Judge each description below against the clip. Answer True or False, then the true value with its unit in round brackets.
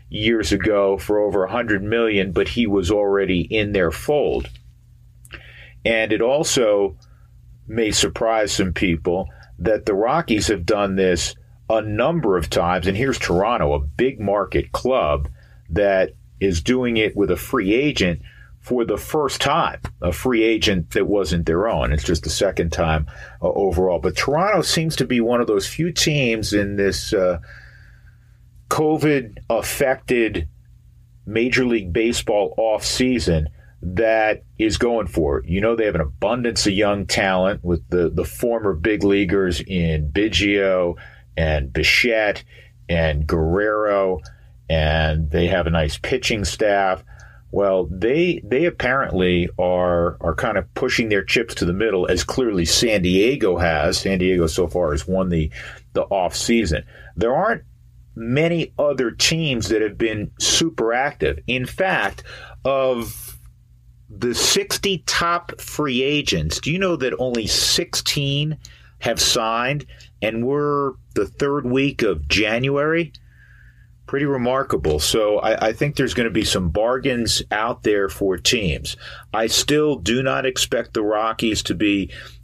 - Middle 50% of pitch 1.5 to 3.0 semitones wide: False (5.1 semitones)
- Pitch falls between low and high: False (105 Hz)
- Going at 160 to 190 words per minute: False (145 wpm)